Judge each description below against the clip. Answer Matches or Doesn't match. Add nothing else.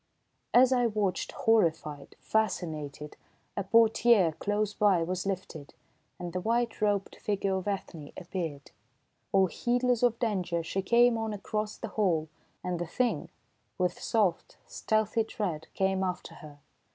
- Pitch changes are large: Doesn't match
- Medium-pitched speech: Doesn't match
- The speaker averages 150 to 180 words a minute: Doesn't match